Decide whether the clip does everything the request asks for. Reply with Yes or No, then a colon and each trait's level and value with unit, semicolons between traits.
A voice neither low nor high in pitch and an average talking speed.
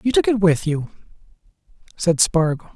Yes: medium, 165 Hz; average, 150 wpm